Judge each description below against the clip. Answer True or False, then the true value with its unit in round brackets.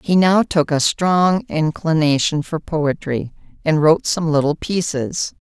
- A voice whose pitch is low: False (160 Hz)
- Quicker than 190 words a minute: False (140 wpm)